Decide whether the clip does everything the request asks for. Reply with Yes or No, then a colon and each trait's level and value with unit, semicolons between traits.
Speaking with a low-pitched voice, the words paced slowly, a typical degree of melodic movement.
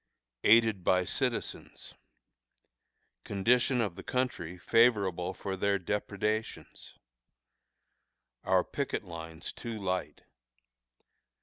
Yes: low, 100 Hz; slow, 85 wpm; average, 3.9 semitones